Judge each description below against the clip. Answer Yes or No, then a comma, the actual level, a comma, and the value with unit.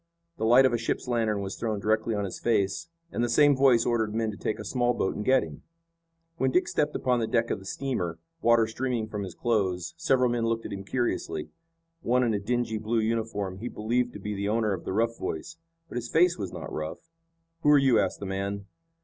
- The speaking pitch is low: Yes, low, 115 Hz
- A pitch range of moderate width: Yes, average, 3.2 semitones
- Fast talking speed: Yes, fast, 235 wpm